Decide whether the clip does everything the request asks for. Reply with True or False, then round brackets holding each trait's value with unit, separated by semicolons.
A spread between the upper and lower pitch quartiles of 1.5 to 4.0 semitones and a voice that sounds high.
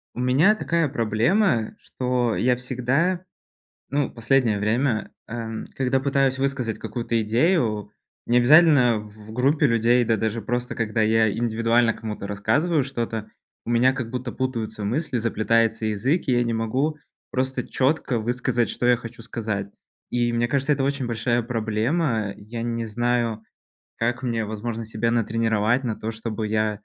False (2.8 semitones; 120 Hz)